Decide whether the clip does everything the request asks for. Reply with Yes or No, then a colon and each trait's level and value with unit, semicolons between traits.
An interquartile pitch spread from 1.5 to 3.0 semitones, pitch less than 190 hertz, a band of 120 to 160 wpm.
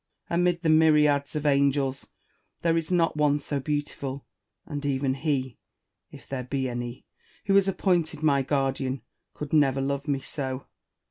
Yes: narrow, 2.6 semitones; medium, 140 Hz; average, 150 wpm